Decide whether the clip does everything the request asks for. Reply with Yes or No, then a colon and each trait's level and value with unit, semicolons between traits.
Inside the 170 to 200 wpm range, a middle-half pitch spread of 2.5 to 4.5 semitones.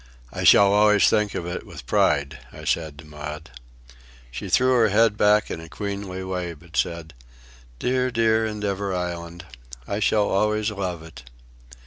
No: average, 160 wpm; average, 4.0 semitones